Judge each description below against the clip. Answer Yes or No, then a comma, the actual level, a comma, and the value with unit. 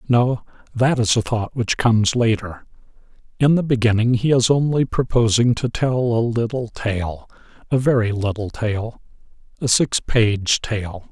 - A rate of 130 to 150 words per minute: Yes, average, 145 wpm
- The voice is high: No, low, 115 Hz